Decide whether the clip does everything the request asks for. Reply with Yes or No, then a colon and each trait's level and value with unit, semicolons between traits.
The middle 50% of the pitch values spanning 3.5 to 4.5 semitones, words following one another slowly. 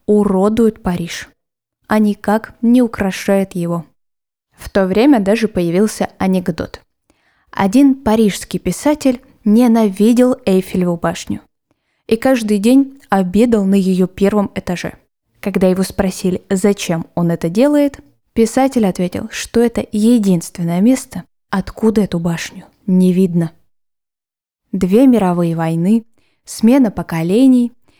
Yes: average, 3.9 semitones; slow, 105 wpm